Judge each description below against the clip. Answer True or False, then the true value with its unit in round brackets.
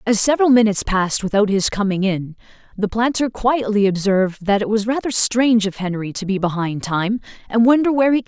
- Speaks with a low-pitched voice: False (215 Hz)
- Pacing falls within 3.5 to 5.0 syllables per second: False (6.1 syllables/s)